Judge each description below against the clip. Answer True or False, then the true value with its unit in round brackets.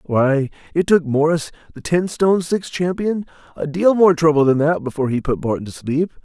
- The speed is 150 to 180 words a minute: False (200 wpm)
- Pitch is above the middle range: False (160 Hz)